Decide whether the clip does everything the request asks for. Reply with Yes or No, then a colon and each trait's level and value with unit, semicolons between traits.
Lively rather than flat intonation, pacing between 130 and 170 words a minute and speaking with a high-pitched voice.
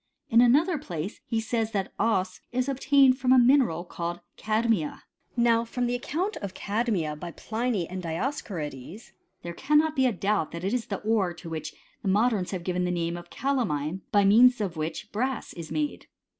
No: wide, 6.1 semitones; average, 185 wpm; high, 215 Hz